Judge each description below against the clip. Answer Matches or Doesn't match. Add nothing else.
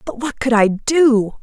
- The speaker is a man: Doesn't match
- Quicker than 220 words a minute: Doesn't match